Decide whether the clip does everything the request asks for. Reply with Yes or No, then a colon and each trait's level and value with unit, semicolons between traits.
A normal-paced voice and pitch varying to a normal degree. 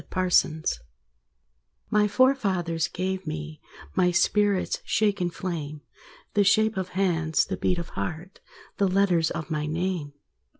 No: slow, 125 wpm; average, 3.3 semitones